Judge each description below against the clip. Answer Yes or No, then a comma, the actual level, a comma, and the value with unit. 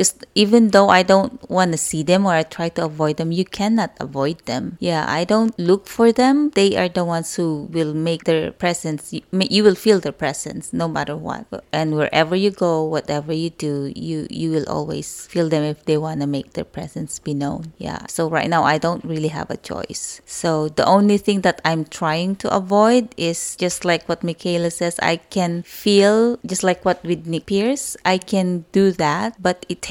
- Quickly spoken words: Yes, fast, 210 wpm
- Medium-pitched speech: Yes, medium, 170 Hz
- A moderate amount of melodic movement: Yes, average, 3.6 semitones